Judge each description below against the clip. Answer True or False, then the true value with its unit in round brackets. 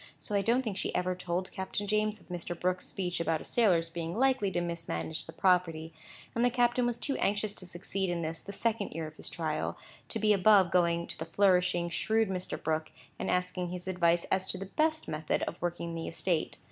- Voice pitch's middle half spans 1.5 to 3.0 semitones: False (3.4 semitones)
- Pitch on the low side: False (180 Hz)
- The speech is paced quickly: True (225 wpm)